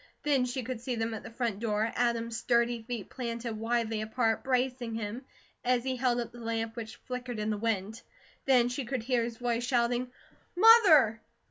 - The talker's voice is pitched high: Yes, high, 235 Hz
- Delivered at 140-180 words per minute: No, average, 190 wpm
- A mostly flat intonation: Yes, narrow, 1.8 semitones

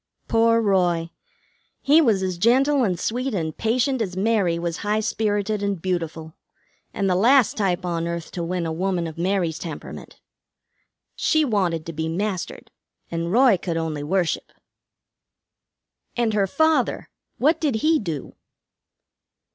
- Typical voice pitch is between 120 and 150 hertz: No, high, 190 Hz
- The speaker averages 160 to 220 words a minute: No, average, 145 wpm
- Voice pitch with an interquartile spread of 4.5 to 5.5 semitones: Yes, average, 5.2 semitones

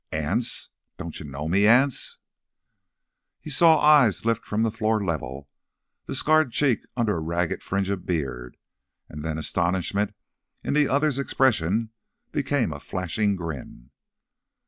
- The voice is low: Yes, low, 100 Hz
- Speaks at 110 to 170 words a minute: Yes, average, 140 wpm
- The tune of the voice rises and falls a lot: Yes, wide, 7.7 semitones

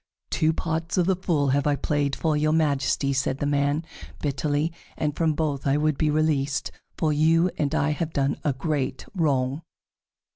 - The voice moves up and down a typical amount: No, narrow, 2.0 semitones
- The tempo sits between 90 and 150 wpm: No, average, 180 wpm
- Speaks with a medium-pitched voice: Yes, medium, 150 Hz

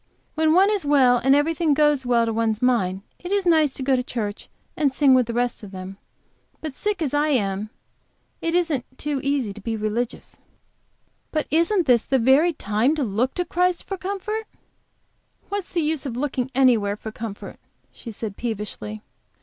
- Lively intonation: Yes, wide, 5.9 semitones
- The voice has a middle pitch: No, very high, 265 Hz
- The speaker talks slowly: No, average, 185 wpm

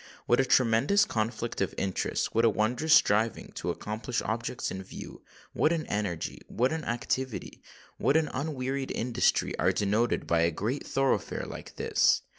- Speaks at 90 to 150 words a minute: Yes, average, 140 wpm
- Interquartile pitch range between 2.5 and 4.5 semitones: Yes, average, 3.8 semitones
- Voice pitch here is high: No, low, 120 Hz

